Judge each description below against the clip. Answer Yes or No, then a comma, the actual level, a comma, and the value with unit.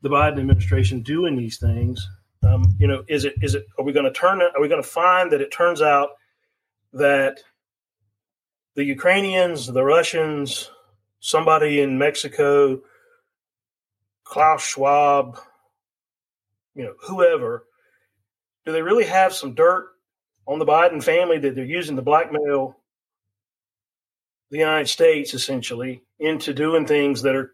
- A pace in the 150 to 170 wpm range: No, average, 140 wpm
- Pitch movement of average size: No, wide, 6.3 semitones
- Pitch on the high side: No, medium, 140 Hz